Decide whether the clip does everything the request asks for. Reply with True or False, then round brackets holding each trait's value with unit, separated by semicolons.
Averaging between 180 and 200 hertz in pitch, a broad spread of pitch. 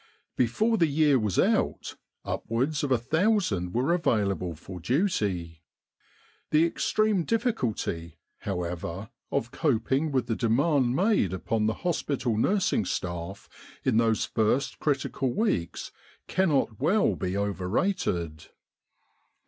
False (120 Hz; 8.4 semitones)